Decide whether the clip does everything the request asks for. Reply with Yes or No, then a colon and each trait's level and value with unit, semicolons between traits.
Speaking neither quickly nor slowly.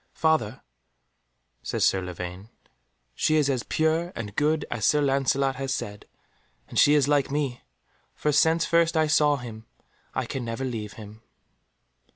Yes: average, 155 wpm